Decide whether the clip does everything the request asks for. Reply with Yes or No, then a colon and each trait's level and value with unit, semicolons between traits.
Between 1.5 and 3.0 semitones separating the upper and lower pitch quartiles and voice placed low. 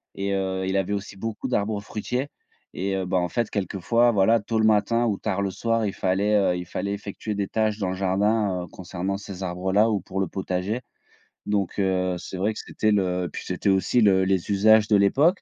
Yes: narrow, 2.4 semitones; low, 100 Hz